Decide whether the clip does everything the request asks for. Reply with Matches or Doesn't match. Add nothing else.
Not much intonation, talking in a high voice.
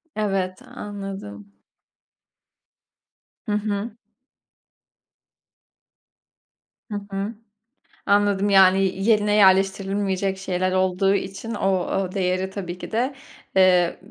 Matches